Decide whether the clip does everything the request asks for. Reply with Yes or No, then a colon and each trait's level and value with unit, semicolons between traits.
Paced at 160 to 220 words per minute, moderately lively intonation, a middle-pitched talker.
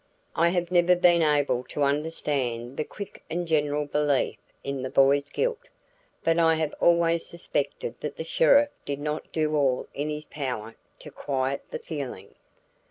Yes: average, 165 wpm; average, 3.4 semitones; medium, 150 Hz